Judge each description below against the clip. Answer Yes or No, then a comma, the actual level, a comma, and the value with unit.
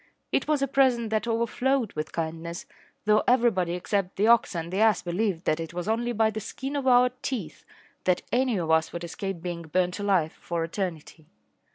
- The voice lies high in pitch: Yes, high, 195 Hz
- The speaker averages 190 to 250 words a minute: Yes, average, 195 wpm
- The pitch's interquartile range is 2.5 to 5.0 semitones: No, wide, 5.6 semitones